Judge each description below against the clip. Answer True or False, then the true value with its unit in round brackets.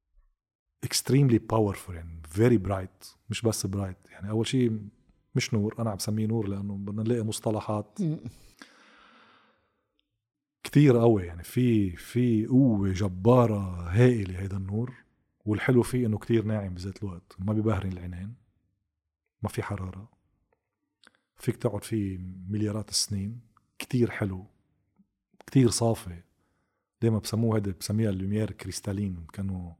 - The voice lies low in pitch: True (105 Hz)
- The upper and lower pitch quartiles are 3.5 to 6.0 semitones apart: False (3.1 semitones)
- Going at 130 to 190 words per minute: False (120 wpm)